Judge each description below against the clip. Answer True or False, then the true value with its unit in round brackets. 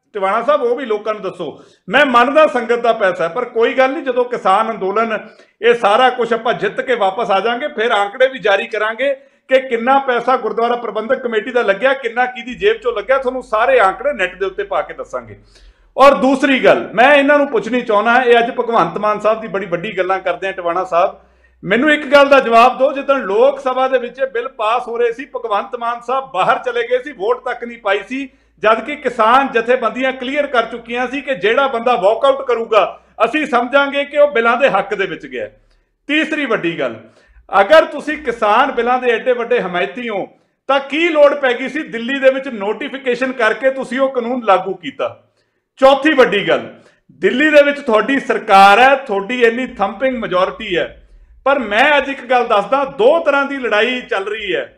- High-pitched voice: True (250 Hz)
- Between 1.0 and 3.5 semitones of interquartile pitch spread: False (3.9 semitones)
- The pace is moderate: False (195 wpm)